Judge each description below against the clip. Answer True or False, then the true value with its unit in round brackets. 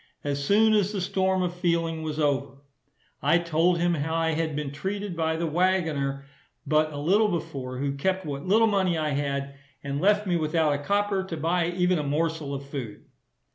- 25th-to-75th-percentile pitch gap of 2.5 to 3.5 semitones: False (4.1 semitones)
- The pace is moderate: True (195 wpm)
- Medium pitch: True (165 Hz)